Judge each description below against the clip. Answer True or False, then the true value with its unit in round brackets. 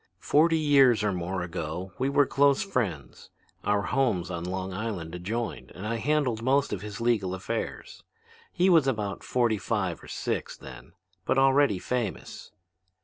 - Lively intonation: True (6.4 semitones)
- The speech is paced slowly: False (155 wpm)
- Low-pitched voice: True (110 Hz)